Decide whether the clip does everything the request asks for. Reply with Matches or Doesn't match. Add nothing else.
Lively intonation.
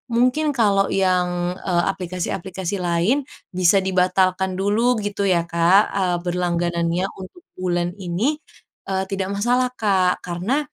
Doesn't match